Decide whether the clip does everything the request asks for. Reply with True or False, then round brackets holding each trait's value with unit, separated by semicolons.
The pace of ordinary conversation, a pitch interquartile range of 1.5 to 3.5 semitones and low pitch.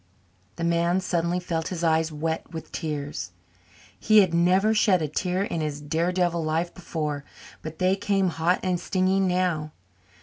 False (160 wpm; 2.5 semitones; 170 Hz)